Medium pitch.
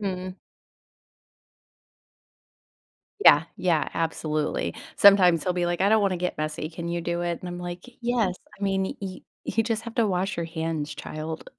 Yes: medium, 180 Hz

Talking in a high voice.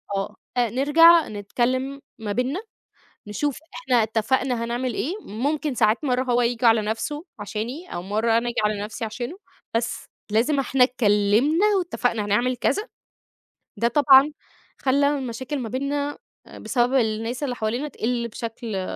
Yes: high, 245 Hz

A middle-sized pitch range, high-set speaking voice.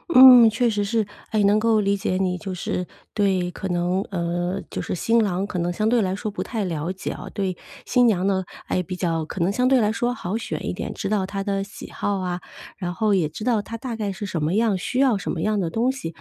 Yes: average, 3.4 semitones; high, 200 Hz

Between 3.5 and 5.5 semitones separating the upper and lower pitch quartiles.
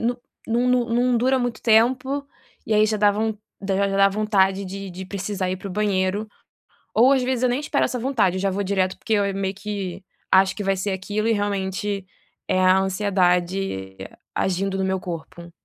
No: average, 2.8 semitones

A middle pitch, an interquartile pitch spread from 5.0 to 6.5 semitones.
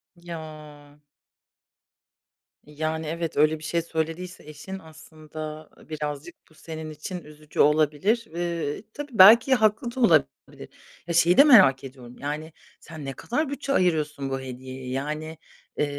No: medium, 155 Hz; average, 2.8 semitones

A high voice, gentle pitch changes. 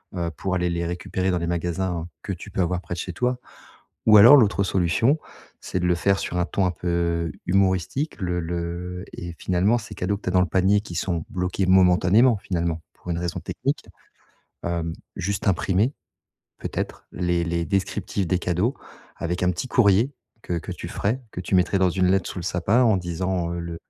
No: very low, 90 Hz; narrow, 2.1 semitones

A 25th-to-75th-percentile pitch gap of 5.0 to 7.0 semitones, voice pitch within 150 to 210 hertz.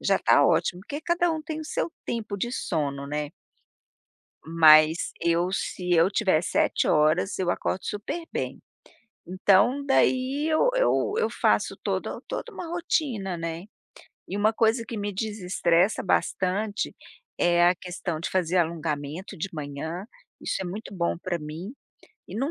Yes: wide, 5.5 semitones; medium, 185 Hz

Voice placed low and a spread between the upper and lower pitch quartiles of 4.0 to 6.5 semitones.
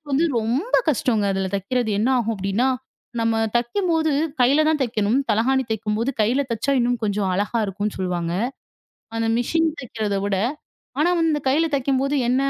No: high, 235 Hz; average, 4.5 semitones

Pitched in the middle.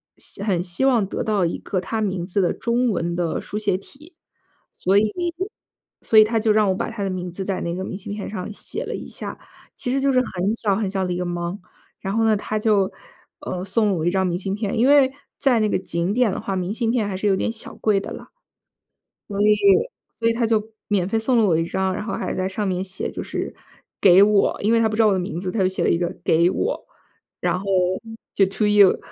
No: high, 200 Hz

